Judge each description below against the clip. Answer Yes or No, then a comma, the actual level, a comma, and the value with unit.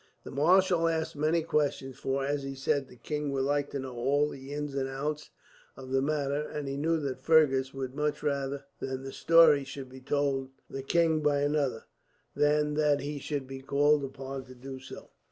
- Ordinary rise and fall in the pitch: No, narrow, 1.9 semitones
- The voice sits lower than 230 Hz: Yes, medium, 140 Hz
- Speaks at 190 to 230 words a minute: Yes, average, 200 wpm